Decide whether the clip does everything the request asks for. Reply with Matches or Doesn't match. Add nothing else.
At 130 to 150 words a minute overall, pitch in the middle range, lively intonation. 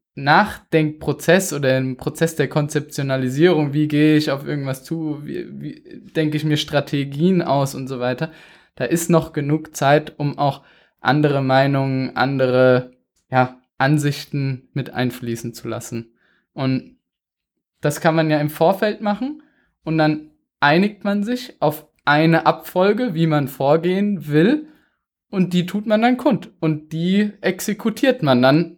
Doesn't match